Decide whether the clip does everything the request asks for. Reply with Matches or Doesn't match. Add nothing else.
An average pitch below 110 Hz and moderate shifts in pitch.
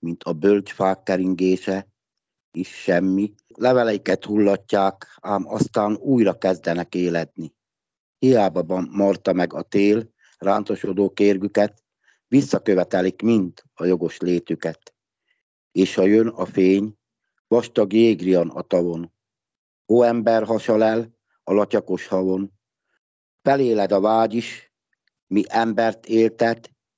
Matches